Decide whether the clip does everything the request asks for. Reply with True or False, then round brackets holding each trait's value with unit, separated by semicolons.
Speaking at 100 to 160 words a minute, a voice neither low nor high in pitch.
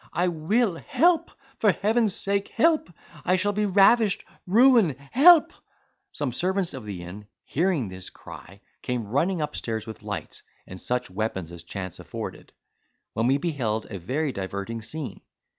True (150 wpm; 150 Hz)